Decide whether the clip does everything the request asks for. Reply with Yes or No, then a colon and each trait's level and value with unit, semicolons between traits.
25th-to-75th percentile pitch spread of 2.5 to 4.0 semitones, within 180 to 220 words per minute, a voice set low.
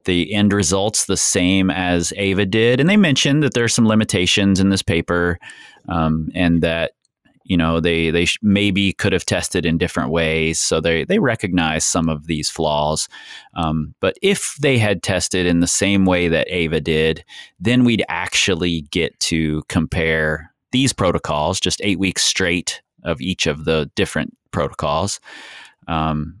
No: average, 3.7 semitones; average, 170 wpm; very low, 90 Hz